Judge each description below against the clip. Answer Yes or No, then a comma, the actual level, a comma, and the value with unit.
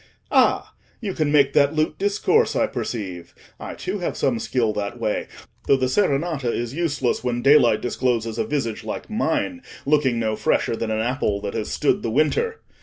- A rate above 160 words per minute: Yes, average, 180 wpm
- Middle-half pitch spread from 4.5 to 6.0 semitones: Yes, average, 5.2 semitones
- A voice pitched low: Yes, low, 130 Hz